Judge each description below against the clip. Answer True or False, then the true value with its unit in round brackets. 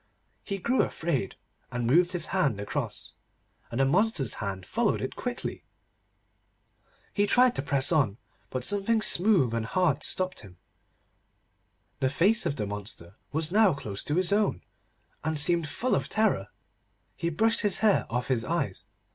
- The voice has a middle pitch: True (155 Hz)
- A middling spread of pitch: False (8.4 semitones)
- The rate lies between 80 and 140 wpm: False (155 wpm)